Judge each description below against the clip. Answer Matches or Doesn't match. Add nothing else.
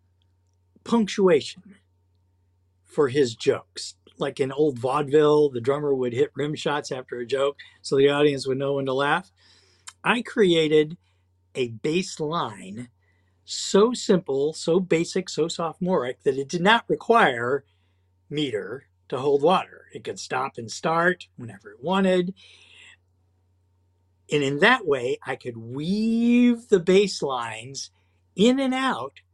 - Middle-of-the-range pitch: Matches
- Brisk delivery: Doesn't match